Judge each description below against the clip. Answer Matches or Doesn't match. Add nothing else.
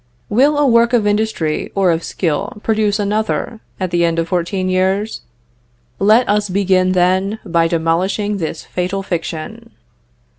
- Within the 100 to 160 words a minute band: Matches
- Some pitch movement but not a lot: Matches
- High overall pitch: Matches